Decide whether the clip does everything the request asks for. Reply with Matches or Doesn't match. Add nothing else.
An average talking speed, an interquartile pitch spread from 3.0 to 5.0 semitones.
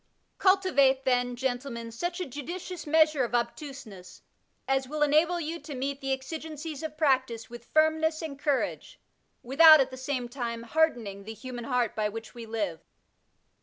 Matches